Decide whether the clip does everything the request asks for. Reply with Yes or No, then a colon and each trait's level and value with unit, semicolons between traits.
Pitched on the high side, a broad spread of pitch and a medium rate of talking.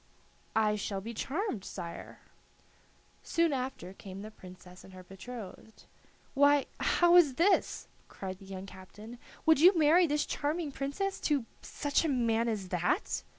Yes: high, 235 Hz; wide, 7.5 semitones; average, 150 wpm